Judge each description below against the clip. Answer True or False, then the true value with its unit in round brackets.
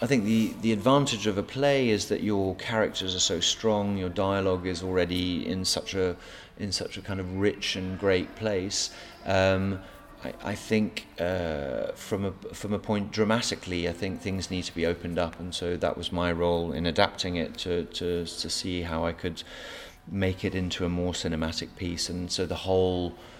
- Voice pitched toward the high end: False (95 Hz)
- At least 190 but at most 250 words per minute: True (195 wpm)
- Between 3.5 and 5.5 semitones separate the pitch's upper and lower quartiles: False (2.5 semitones)